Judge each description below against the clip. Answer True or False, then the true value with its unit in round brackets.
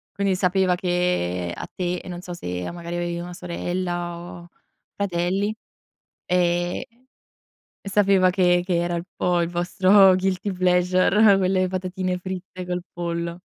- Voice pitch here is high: False (180 Hz)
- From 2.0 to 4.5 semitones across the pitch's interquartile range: False (1.2 semitones)